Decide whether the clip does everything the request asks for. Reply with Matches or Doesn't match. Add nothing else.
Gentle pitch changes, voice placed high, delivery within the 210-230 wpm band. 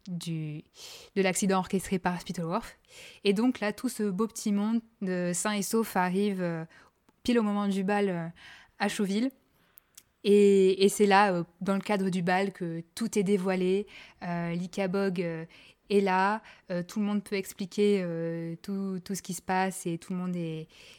Doesn't match